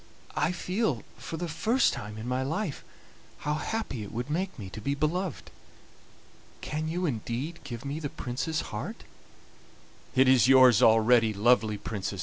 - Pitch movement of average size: No, wide, 5.7 semitones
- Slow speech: No, average, 155 wpm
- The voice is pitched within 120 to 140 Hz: Yes, low, 135 Hz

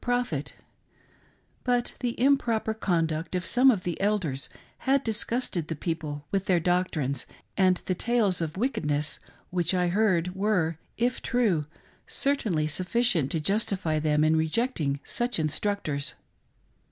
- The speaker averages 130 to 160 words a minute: Yes, slow, 135 wpm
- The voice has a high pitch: No, medium, 180 Hz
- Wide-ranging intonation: Yes, wide, 6.2 semitones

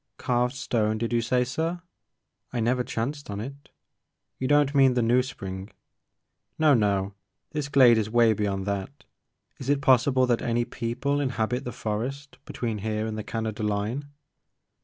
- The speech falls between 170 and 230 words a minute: Yes, average, 175 wpm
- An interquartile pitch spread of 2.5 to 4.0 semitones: Yes, average, 3.6 semitones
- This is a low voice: Yes, low, 120 Hz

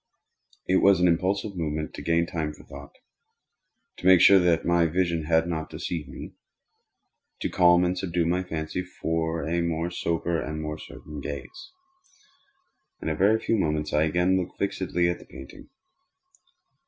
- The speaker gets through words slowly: No, average, 155 wpm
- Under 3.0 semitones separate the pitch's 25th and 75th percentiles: Yes, narrow, 2.4 semitones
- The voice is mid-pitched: No, very low, 85 Hz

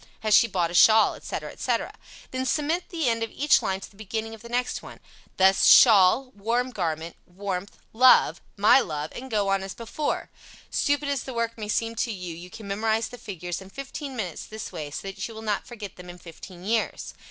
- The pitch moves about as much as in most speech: Yes, average, 4.2 semitones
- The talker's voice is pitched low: No, high, 215 Hz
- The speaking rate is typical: No, fast, 215 wpm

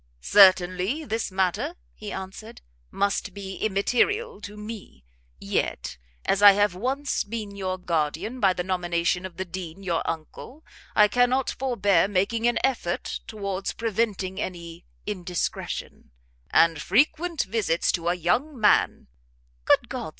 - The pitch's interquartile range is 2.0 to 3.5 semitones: No, average, 4.3 semitones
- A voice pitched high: Yes, high, 195 Hz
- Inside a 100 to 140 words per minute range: Yes, slow, 135 wpm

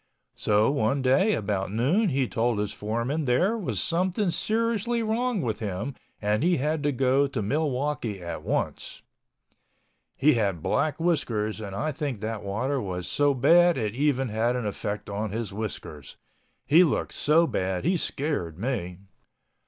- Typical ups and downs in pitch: No, wide, 6.8 semitones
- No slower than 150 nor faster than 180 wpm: Yes, average, 160 wpm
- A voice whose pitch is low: Yes, low, 130 Hz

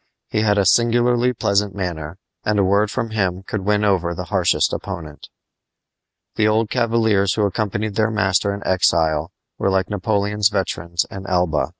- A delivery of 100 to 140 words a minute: No, average, 165 wpm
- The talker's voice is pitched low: Yes, low, 100 Hz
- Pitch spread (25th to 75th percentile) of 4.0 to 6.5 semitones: No, average, 2.7 semitones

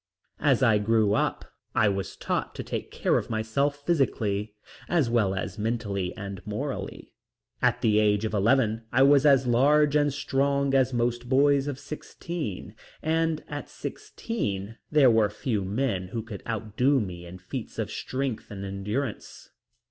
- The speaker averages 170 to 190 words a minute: No, average, 155 wpm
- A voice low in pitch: Yes, low, 115 Hz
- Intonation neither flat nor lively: Yes, average, 5.0 semitones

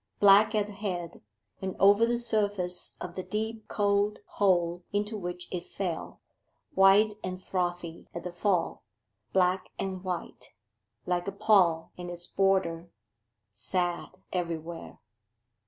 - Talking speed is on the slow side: Yes, slow, 130 wpm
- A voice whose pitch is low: No, medium, 185 Hz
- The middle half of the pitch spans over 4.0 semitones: No, narrow, 2.5 semitones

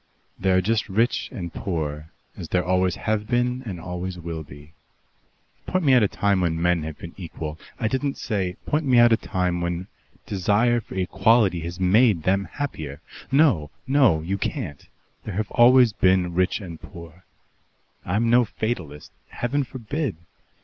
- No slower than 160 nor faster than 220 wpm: Yes, average, 170 wpm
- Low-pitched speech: Yes, very low, 95 Hz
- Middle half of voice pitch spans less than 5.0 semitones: No, wide, 5.5 semitones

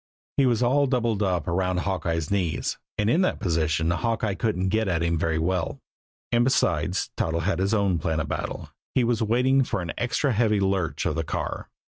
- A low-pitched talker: Yes, very low, 95 Hz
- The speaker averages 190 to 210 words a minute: Yes, average, 195 wpm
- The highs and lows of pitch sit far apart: Yes, wide, 5.7 semitones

